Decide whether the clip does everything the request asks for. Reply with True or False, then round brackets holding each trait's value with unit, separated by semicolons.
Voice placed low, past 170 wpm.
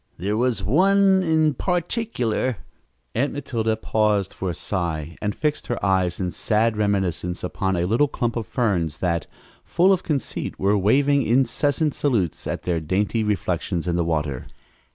False (105 Hz; 160 wpm)